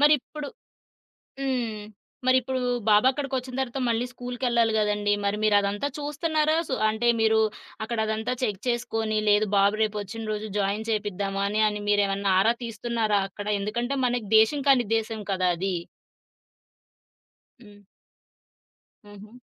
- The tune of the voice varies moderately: Yes, average, 3.2 semitones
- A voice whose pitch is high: Yes, high, 220 Hz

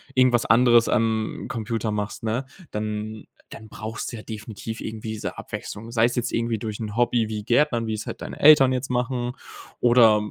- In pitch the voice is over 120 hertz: No, low, 115 Hz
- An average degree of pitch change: No, narrow, 2.0 semitones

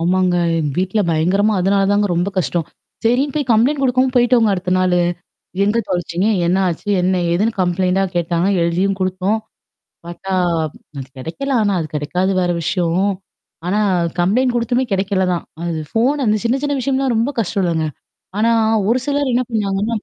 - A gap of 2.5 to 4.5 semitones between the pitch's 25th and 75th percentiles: No, average, 4.9 semitones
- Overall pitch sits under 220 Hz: Yes, high, 195 Hz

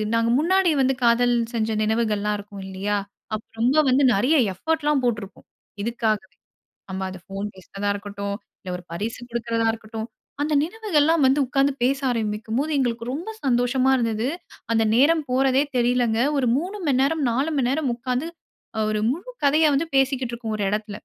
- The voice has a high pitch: Yes, high, 240 Hz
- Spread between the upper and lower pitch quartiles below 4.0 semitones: No, average, 4.3 semitones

